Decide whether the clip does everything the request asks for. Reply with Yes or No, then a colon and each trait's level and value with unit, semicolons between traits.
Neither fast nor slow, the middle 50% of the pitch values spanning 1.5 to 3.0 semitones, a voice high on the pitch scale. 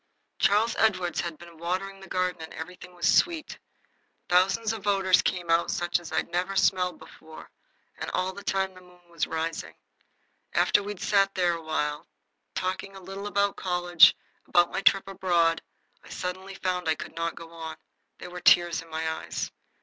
No: average, 180 wpm; narrow, 2.4 semitones; medium, 180 Hz